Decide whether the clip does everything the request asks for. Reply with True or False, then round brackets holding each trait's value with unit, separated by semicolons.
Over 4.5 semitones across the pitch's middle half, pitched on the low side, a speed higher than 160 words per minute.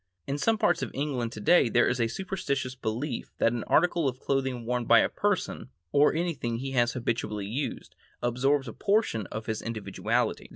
False (3.7 semitones; 125 Hz; 180 wpm)